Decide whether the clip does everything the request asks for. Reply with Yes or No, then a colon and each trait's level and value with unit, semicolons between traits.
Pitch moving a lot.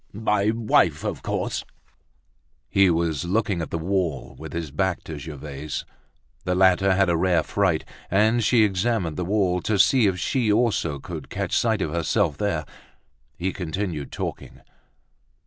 No: average, 3.9 semitones